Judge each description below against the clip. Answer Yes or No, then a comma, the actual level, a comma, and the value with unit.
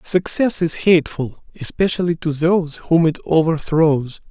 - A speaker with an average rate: No, slow, 125 wpm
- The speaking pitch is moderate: Yes, medium, 165 Hz